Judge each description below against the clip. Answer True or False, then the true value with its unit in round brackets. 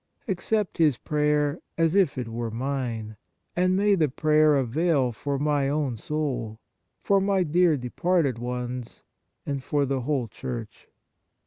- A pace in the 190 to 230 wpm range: False (140 wpm)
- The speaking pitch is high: False (145 Hz)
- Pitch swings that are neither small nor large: True (4.8 semitones)